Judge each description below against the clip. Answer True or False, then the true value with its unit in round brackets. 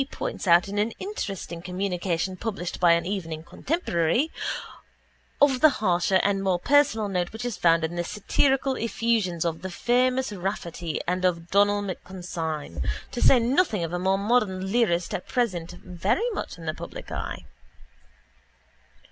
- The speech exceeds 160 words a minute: False (155 wpm)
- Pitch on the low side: False (190 Hz)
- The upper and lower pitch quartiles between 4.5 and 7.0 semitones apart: True (5.0 semitones)